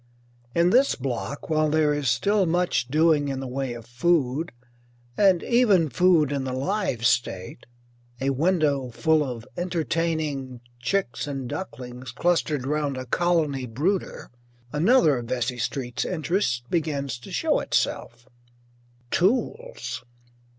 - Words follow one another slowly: Yes, slow, 130 wpm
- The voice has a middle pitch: Yes, medium, 145 Hz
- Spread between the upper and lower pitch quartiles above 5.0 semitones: Yes, wide, 5.4 semitones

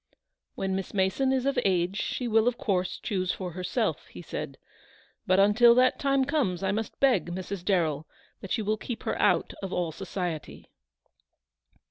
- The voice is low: No, high, 195 Hz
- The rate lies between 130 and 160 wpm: No, average, 175 wpm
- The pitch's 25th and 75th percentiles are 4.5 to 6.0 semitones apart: Yes, average, 4.8 semitones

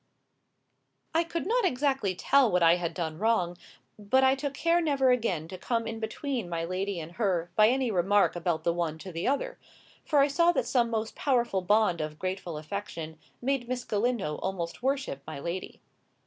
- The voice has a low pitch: No, high, 210 Hz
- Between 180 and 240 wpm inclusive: Yes, average, 190 wpm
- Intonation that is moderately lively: No, wide, 7.3 semitones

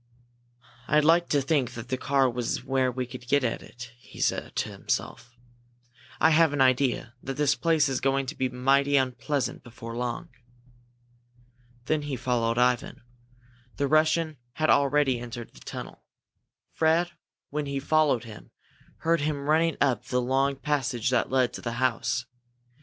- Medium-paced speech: Yes, average, 165 wpm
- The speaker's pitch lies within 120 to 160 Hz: Yes, low, 135 Hz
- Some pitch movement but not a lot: Yes, average, 3.2 semitones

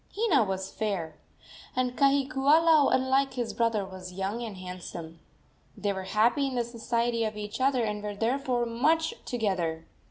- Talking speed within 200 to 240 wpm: No, average, 155 wpm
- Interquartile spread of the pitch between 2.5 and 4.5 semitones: No, average, 5.3 semitones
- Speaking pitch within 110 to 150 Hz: No, high, 230 Hz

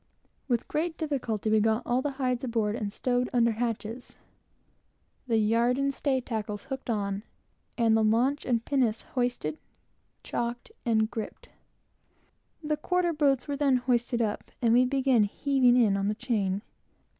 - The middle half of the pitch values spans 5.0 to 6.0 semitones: No, average, 3.4 semitones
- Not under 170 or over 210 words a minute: No, average, 155 wpm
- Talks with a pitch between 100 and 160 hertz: No, high, 240 Hz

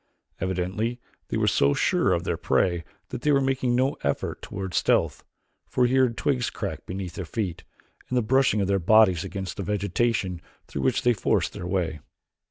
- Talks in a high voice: No, low, 100 Hz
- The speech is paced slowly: No, average, 185 wpm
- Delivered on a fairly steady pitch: No, average, 5.3 semitones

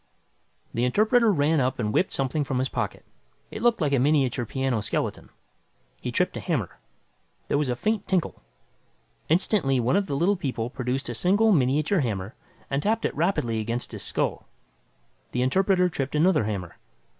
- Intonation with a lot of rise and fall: Yes, wide, 6.9 semitones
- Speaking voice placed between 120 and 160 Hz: Yes, medium, 140 Hz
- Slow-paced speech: No, average, 170 wpm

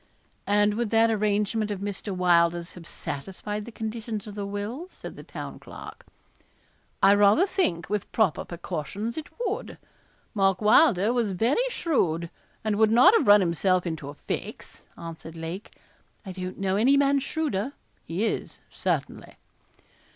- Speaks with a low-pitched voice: No, high, 205 Hz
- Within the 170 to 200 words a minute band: No, average, 150 wpm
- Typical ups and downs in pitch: Yes, average, 3.9 semitones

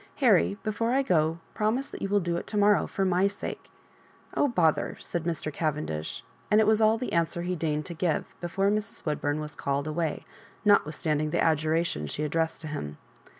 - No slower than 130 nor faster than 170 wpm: No, average, 200 wpm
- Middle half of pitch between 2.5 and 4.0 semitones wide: No, average, 4.9 semitones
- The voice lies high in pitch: No, medium, 170 Hz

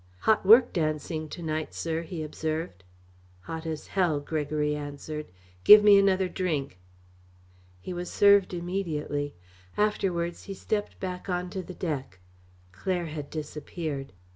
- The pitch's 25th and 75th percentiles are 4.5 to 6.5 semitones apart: No, average, 3.6 semitones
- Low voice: No, medium, 165 Hz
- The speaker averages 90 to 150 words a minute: Yes, slow, 135 wpm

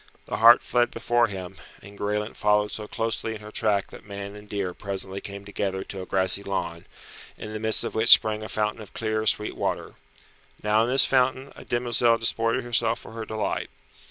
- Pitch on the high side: No, low, 105 Hz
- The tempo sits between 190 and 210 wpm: Yes, average, 200 wpm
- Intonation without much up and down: Yes, narrow, 2.3 semitones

